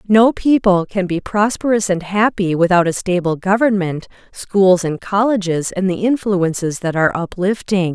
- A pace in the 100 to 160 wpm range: Yes, average, 150 wpm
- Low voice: No, high, 190 Hz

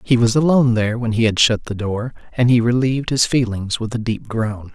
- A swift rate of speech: Yes, fast, 230 wpm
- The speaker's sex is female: No, male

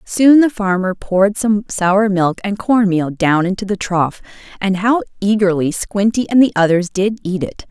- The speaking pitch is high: Yes, high, 200 Hz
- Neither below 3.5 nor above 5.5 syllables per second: Yes, 4.5 syllables/s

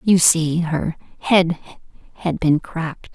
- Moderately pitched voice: Yes, medium, 165 Hz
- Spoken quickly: No, slow, 135 wpm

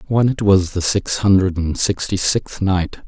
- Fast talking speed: No, average, 195 wpm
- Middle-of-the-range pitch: No, very low, 95 Hz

